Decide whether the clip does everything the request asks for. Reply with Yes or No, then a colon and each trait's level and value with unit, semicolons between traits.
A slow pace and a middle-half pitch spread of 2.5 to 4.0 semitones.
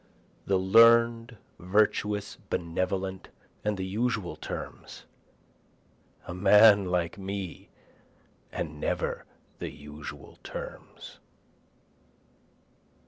Yes: slow, 80 wpm; average, 2.8 semitones